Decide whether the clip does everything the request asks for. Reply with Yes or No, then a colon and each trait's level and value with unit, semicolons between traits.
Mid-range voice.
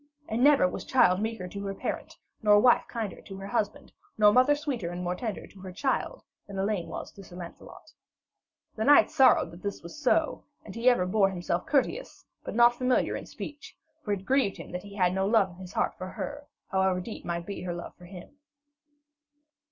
No: high, 200 Hz